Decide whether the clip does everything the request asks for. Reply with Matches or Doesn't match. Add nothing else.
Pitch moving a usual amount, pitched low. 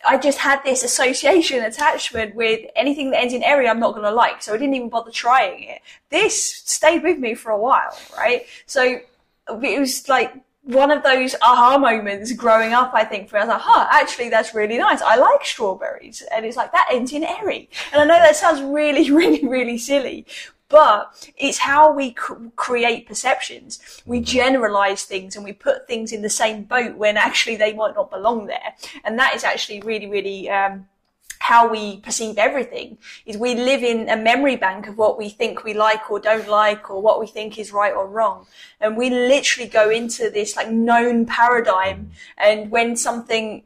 Doesn't match